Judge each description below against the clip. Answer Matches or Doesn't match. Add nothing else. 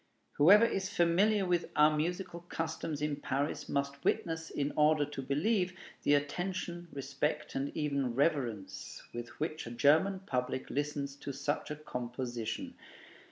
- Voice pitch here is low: Doesn't match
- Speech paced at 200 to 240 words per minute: Doesn't match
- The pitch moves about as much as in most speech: Matches